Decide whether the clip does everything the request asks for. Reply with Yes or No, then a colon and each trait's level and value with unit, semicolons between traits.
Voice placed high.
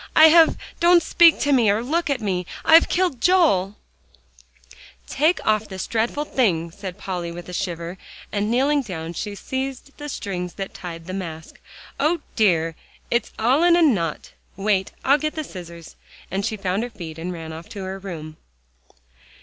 Yes: high, 205 Hz